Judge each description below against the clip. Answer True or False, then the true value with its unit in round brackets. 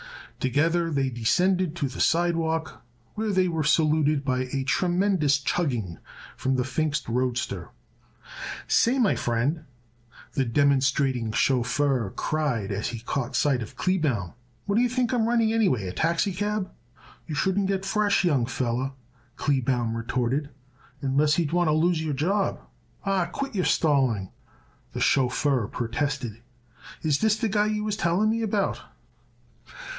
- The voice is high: False (150 Hz)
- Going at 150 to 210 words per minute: False (140 wpm)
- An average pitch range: False (6.5 semitones)